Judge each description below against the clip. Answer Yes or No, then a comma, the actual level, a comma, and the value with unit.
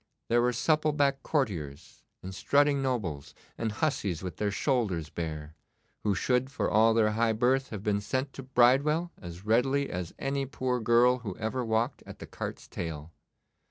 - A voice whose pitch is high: No, low, 115 Hz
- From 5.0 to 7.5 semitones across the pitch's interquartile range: Yes, wide, 5.6 semitones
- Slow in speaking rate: No, average, 170 wpm